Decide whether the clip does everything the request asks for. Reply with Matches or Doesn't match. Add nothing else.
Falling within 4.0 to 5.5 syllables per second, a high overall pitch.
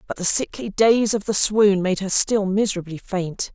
Matches